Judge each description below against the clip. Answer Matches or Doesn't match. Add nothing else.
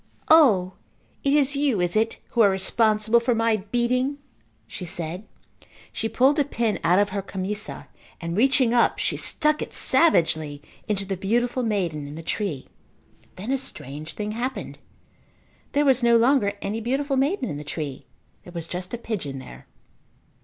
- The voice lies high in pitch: Matches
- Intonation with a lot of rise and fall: Matches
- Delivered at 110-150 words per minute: Doesn't match